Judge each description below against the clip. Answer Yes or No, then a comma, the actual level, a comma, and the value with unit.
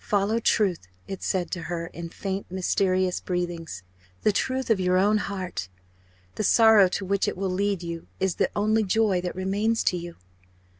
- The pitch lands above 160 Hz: Yes, high, 190 Hz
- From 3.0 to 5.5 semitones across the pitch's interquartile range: No, narrow, 2.5 semitones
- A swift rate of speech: No, average, 180 wpm